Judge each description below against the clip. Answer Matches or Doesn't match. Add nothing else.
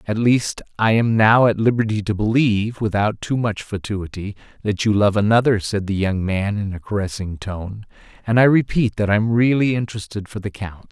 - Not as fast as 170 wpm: Doesn't match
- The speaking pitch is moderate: Doesn't match